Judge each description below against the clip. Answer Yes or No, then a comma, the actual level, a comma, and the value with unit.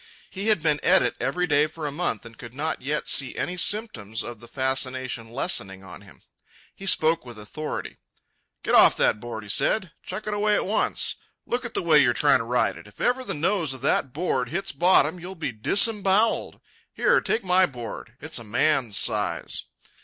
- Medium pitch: Yes, medium, 150 Hz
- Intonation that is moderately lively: No, wide, 7.7 semitones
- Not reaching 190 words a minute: No, average, 200 wpm